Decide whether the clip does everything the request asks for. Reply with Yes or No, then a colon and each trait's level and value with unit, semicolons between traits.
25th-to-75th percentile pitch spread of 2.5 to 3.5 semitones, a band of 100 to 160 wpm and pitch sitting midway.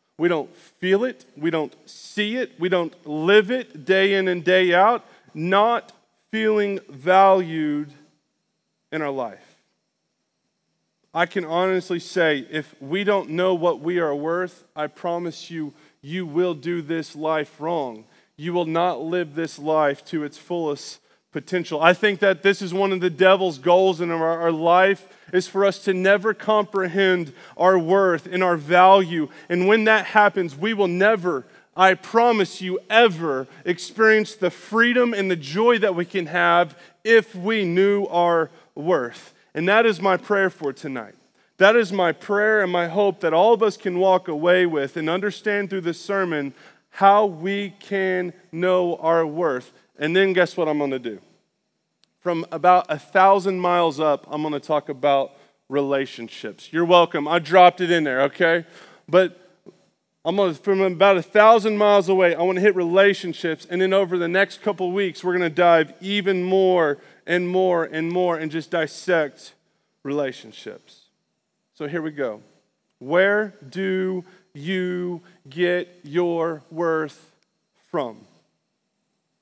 Yes: average, 3.0 semitones; average, 155 wpm; medium, 180 Hz